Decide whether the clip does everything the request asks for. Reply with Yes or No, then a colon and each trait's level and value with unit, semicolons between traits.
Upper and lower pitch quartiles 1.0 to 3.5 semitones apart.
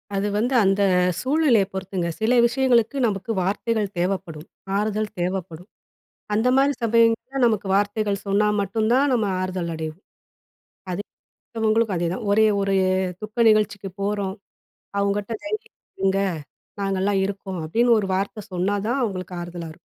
Yes: average, 3.0 semitones